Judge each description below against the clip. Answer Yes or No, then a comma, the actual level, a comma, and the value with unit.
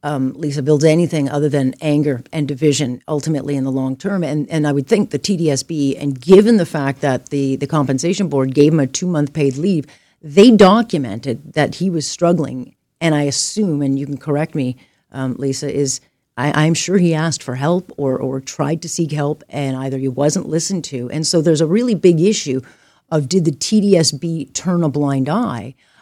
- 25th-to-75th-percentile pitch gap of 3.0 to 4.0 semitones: Yes, average, 3.4 semitones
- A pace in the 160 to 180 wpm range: No, fast, 205 wpm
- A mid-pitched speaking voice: Yes, medium, 150 Hz